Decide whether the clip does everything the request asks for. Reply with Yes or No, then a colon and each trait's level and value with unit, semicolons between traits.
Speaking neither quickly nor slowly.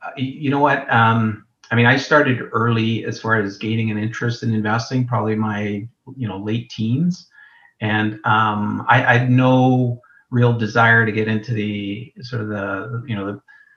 Yes: average, 180 wpm